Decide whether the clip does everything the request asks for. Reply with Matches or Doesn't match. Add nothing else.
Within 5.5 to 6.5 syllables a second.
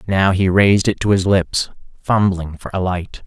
Doesn't match